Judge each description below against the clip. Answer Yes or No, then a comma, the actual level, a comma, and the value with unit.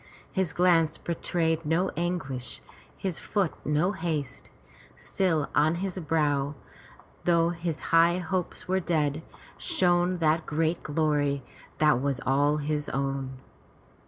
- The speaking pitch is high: No, medium, 160 Hz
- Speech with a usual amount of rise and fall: Yes, average, 3.1 semitones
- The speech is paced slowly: Yes, slow, 120 wpm